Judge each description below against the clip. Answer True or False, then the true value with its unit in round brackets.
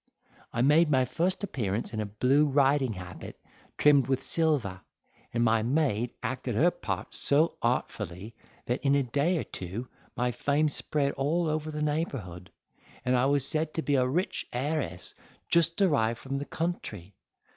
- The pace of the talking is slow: False (165 wpm)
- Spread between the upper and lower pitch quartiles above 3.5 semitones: True (4.6 semitones)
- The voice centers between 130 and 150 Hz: True (135 Hz)